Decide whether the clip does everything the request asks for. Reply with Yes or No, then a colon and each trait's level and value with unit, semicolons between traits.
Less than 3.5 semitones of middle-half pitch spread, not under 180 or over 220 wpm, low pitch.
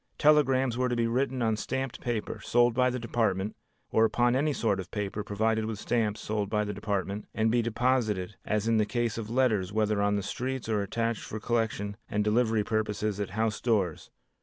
Yes: narrow, 2.5 semitones; average, 200 wpm; low, 110 Hz